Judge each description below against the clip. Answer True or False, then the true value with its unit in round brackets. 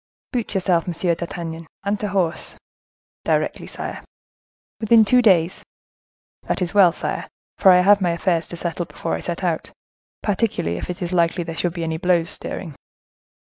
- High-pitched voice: False (175 Hz)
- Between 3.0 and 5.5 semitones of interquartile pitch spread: False (2.6 semitones)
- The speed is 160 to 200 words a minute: True (170 wpm)